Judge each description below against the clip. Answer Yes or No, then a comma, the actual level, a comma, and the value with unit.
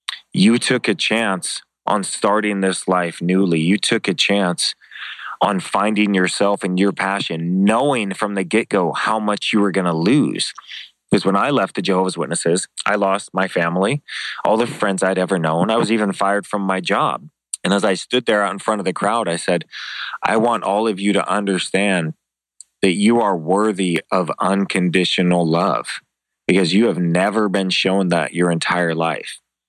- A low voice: Yes, very low, 95 Hz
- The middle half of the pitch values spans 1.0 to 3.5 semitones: Yes, narrow, 2.6 semitones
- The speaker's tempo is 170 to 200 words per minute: Yes, average, 185 wpm